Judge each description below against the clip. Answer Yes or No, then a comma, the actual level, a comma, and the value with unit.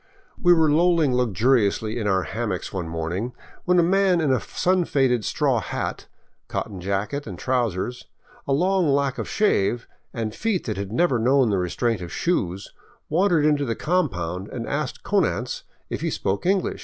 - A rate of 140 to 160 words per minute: No, average, 175 wpm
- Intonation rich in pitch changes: Yes, wide, 8.8 semitones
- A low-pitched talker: Yes, low, 125 Hz